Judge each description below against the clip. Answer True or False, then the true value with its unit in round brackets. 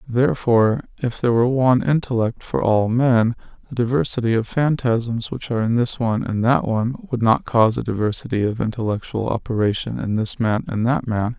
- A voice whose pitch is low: True (115 Hz)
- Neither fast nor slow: True (185 wpm)